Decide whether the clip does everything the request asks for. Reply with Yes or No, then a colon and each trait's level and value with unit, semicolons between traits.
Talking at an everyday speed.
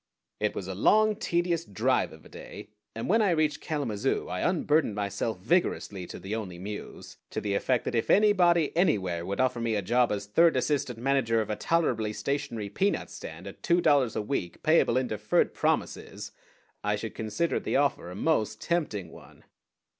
Yes: average, 185 wpm